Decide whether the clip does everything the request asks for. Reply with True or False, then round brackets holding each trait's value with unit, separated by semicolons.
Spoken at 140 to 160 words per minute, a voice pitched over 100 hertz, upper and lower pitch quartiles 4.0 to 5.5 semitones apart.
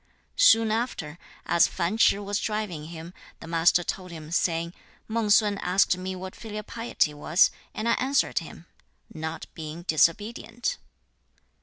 True (150 wpm; 185 Hz; 4.6 semitones)